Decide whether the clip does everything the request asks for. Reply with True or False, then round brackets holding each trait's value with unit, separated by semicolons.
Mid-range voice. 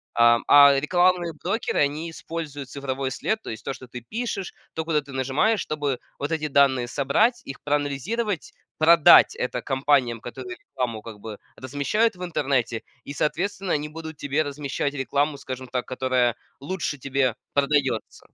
True (145 Hz)